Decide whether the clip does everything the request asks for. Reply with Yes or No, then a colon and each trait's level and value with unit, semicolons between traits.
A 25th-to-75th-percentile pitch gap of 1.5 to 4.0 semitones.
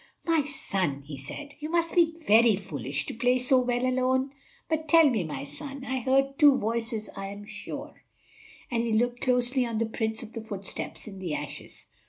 No: average, 5.1 semitones